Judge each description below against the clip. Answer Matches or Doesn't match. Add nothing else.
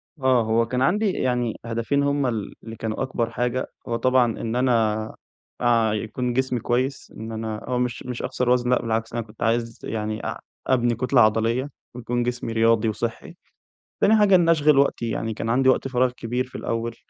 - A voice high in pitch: Doesn't match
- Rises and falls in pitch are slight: Matches